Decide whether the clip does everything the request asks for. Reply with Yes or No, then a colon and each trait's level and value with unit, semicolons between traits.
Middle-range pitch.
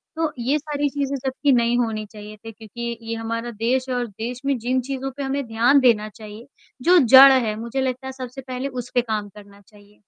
No: high, 245 Hz